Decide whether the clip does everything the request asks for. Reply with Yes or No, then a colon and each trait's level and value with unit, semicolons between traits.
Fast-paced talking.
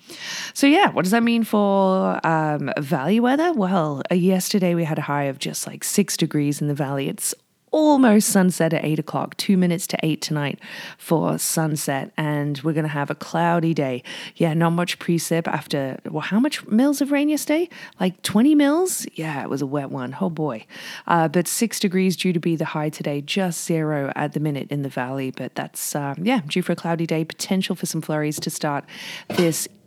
Yes: fast, 210 wpm